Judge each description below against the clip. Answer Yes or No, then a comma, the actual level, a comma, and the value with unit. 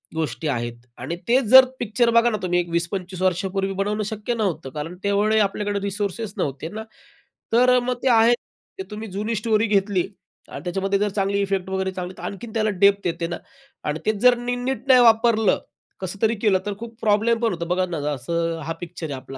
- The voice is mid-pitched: No, high, 200 Hz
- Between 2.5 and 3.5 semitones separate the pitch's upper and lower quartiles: No, average, 4.0 semitones